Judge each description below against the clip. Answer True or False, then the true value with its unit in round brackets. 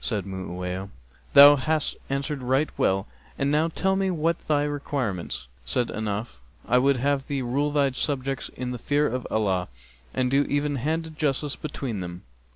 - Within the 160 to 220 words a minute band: True (170 wpm)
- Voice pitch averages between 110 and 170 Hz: True (135 Hz)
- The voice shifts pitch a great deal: False (5.0 semitones)